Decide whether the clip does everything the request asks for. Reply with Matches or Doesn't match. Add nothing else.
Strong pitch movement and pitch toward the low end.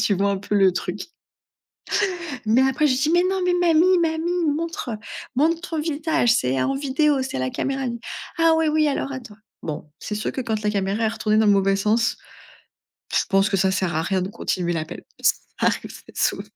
Doesn't match